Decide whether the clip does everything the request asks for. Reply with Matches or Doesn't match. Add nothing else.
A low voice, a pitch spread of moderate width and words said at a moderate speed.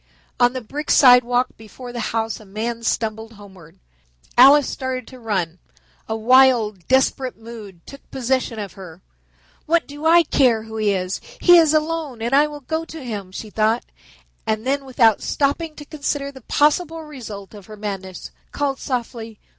Doesn't match